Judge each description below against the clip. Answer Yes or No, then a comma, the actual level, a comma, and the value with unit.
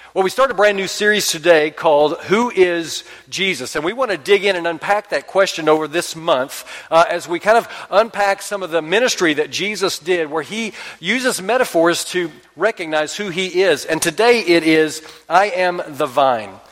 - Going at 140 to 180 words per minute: No, average, 195 wpm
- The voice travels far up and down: No, average, 4.1 semitones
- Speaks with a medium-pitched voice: Yes, medium, 180 Hz